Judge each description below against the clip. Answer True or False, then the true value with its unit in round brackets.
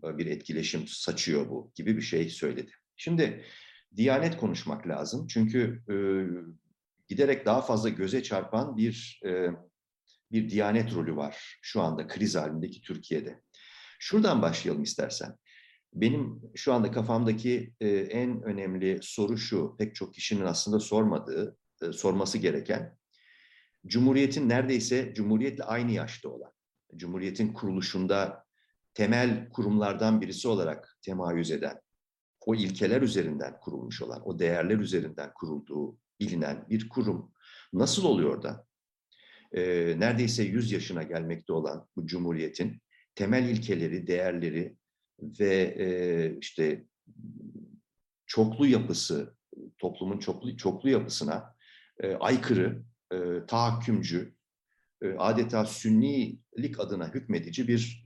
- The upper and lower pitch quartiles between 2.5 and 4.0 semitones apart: False (4.5 semitones)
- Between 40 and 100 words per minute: False (115 wpm)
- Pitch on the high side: False (110 Hz)